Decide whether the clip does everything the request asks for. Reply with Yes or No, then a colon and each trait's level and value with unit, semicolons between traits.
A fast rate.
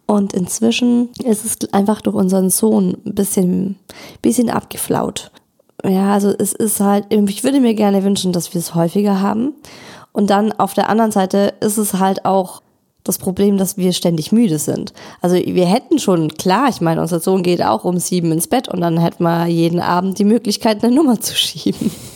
Yes: fast, 195 wpm